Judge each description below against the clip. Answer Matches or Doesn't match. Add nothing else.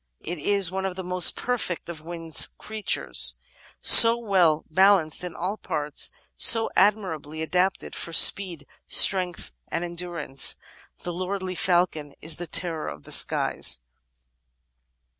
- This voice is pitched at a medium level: Matches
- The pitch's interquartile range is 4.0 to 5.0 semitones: Doesn't match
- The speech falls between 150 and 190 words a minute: Doesn't match